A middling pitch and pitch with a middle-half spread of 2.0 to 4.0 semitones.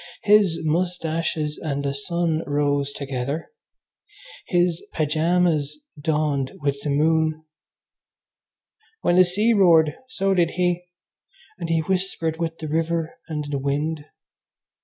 Yes: medium, 160 Hz; average, 2.9 semitones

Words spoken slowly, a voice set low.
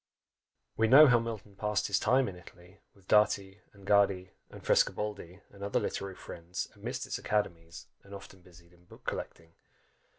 No: average, 165 wpm; low, 100 Hz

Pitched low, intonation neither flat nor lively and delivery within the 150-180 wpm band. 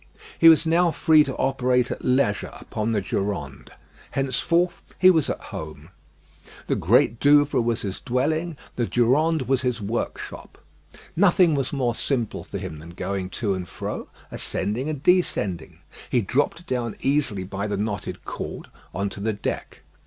No: low, 125 Hz; wide, 6.5 semitones; average, 160 wpm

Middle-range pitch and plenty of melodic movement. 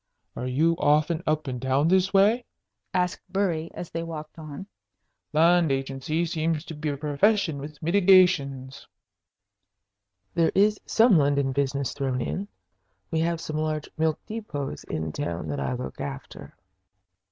No: medium, 155 Hz; average, 3.9 semitones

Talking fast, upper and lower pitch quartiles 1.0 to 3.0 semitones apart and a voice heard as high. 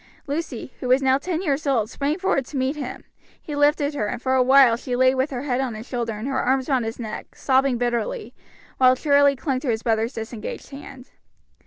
Yes: fast, 215 wpm; narrow, 2.5 semitones; very high, 260 Hz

